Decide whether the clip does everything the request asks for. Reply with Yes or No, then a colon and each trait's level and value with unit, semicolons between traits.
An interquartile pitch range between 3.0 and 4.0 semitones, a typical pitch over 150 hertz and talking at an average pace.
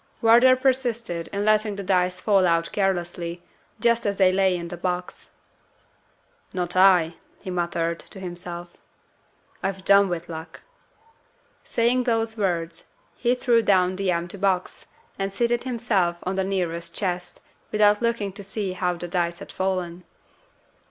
Yes: average, 3.3 semitones; high, 190 Hz; average, 145 wpm